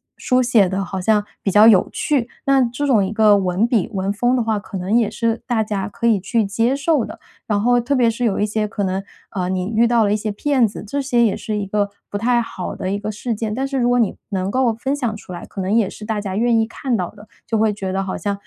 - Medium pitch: No, high, 215 Hz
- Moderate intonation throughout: Yes, average, 3.0 semitones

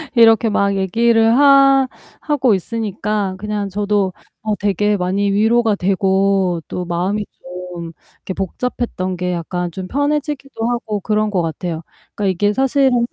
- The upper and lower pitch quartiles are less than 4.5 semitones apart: Yes, average, 3.8 semitones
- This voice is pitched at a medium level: No, high, 205 Hz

